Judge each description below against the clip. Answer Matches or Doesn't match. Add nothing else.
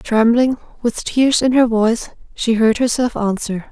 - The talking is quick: Doesn't match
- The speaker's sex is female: Matches